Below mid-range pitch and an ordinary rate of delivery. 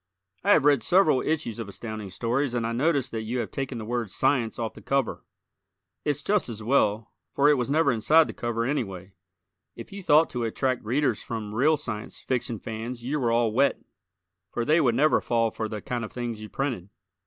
No: low, 120 Hz; fast, 210 wpm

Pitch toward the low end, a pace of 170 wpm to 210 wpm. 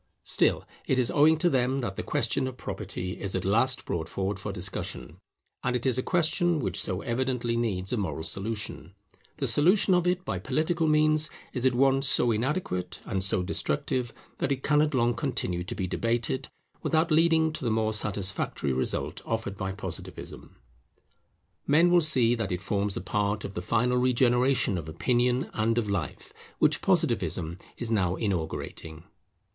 Yes: low, 120 Hz; average, 175 wpm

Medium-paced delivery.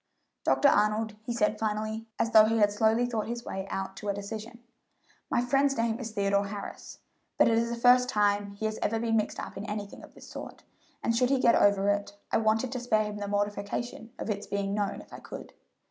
No: fast, 225 wpm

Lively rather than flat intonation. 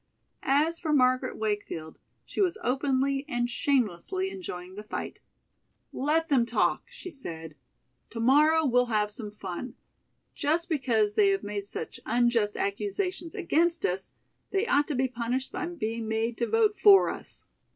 Yes: wide, 7.2 semitones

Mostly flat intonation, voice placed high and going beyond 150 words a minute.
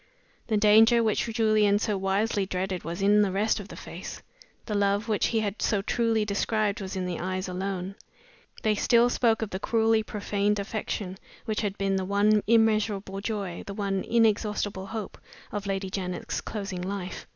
Yes: narrow, 2.0 semitones; high, 205 Hz; average, 175 wpm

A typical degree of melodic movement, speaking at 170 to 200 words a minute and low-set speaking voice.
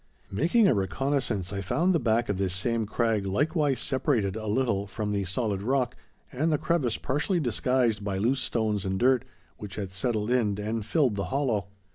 Yes: average, 4.8 semitones; average, 185 wpm; low, 115 Hz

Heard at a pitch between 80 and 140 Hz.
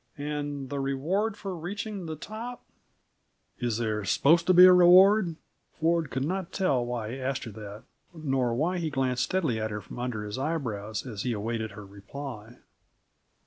Yes: low, 135 Hz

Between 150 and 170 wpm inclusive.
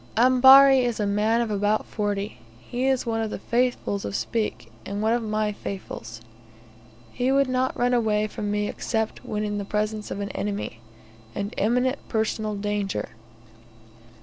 Yes: average, 165 wpm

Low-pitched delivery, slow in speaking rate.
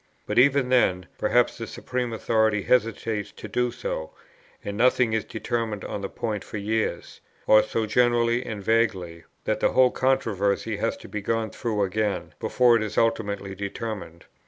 No: low, 110 Hz; average, 165 wpm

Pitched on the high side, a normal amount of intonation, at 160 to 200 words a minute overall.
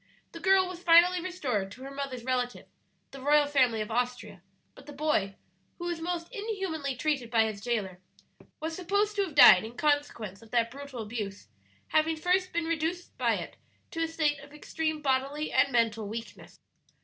No: very high, 285 Hz; wide, 5.9 semitones; average, 180 wpm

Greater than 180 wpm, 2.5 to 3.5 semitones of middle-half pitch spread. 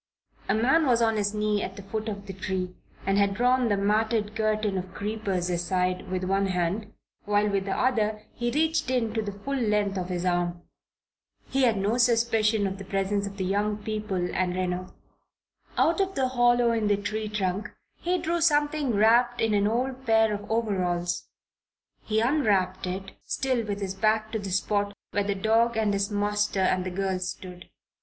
Yes: average, 190 wpm; average, 2.9 semitones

